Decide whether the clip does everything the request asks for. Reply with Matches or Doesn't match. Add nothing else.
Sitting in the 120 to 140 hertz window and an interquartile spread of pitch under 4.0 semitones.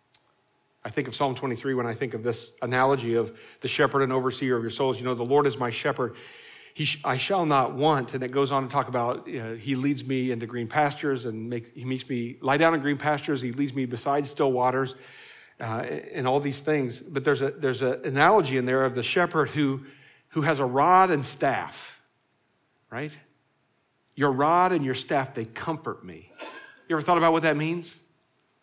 Matches